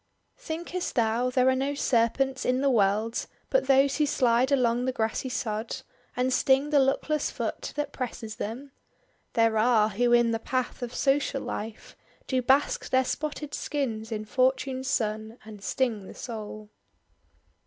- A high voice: Yes, very high, 250 Hz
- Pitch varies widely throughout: No, average, 3.3 semitones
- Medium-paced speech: Yes, average, 155 wpm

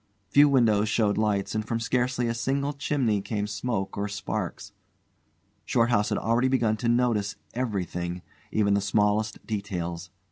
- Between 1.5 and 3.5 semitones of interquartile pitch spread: Yes, average, 3.0 semitones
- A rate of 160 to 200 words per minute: No, average, 145 wpm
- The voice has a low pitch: Yes, low, 110 Hz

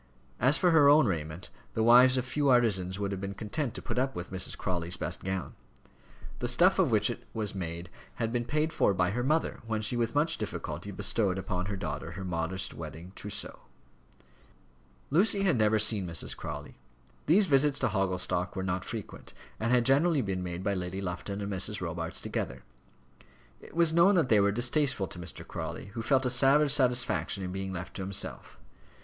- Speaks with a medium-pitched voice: No, low, 105 Hz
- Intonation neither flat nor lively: No, wide, 6.0 semitones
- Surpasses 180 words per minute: Yes, average, 195 wpm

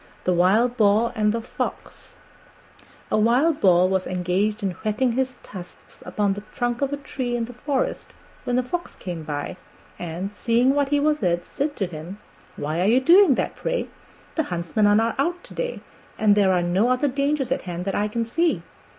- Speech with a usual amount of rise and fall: No, wide, 6.1 semitones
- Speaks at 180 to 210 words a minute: Yes, average, 200 wpm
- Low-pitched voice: No, high, 225 Hz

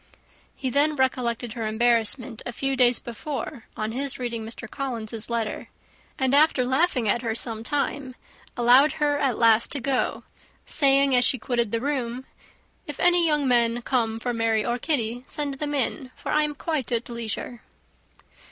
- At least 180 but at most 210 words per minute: No, average, 170 wpm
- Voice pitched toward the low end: No, very high, 250 Hz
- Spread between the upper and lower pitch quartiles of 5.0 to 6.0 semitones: No, average, 3.2 semitones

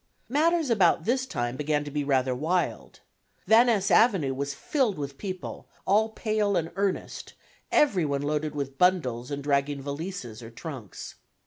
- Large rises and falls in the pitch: Yes, wide, 6.5 semitones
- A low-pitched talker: No, medium, 155 Hz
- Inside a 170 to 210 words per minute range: No, average, 155 wpm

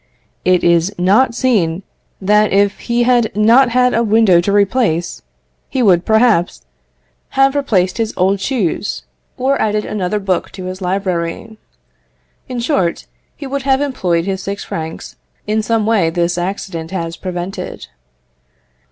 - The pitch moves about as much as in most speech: Yes, average, 4.7 semitones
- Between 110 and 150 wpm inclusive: Yes, average, 145 wpm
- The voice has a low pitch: No, high, 200 Hz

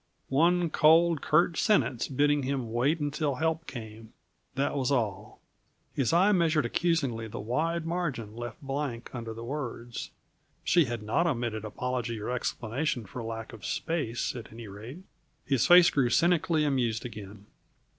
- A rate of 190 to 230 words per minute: No, average, 150 wpm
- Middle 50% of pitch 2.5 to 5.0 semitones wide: No, wide, 5.6 semitones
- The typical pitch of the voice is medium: No, low, 130 Hz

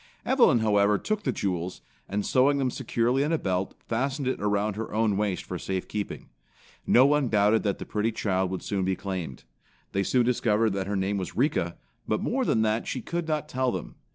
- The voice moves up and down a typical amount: Yes, average, 4.8 semitones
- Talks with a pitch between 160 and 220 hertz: No, low, 110 Hz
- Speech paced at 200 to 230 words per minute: Yes, fast, 205 wpm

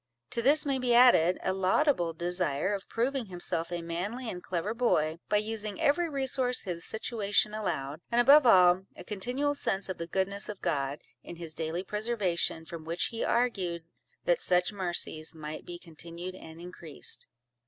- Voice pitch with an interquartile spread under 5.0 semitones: No, wide, 5.6 semitones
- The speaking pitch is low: No, high, 190 Hz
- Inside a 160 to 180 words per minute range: Yes, average, 170 wpm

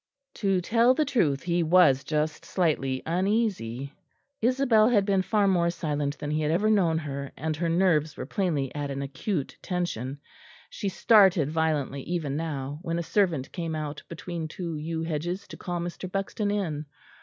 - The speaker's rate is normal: Yes, average, 170 wpm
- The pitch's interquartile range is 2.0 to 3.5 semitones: No, average, 4.5 semitones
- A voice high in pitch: No, medium, 165 Hz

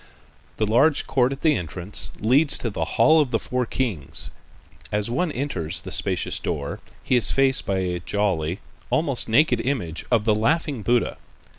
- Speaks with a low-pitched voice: Yes, low, 115 Hz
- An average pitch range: No, wide, 5.7 semitones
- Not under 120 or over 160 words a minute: No, average, 170 wpm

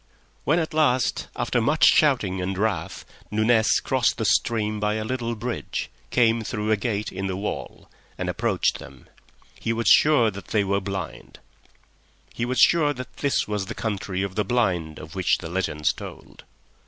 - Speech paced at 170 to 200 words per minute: Yes, average, 175 wpm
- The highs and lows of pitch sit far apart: No, average, 4.0 semitones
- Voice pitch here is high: No, low, 110 Hz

